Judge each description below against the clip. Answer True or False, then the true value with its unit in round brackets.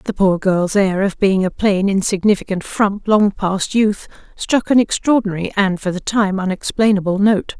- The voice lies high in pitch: True (200 Hz)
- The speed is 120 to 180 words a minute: True (175 wpm)